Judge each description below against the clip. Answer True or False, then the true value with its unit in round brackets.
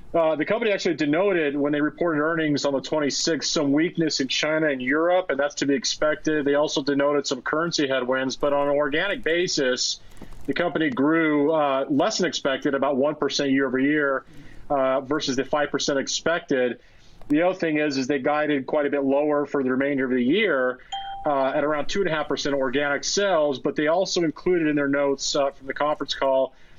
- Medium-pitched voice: True (145 Hz)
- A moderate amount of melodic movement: False (2.2 semitones)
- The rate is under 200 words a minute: False (205 wpm)